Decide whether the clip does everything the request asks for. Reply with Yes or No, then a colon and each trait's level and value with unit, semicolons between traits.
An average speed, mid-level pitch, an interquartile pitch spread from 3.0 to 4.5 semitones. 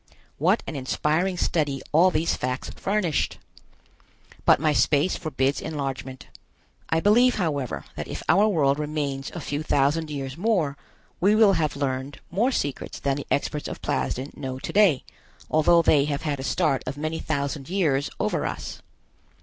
Yes: average, 160 wpm; medium, 150 Hz; average, 3.8 semitones